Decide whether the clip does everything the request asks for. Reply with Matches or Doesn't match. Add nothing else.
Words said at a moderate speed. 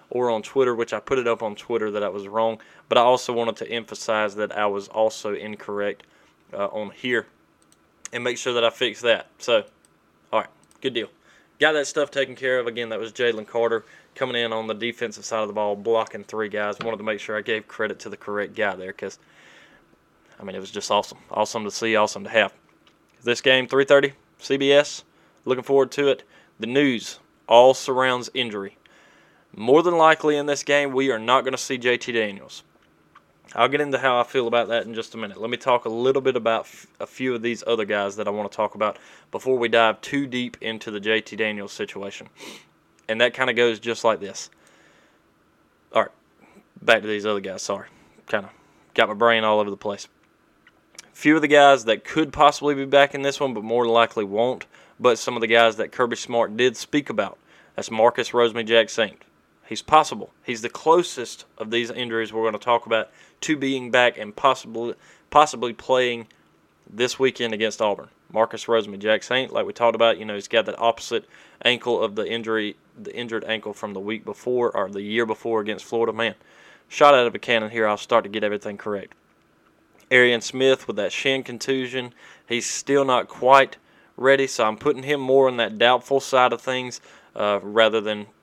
Doesn't match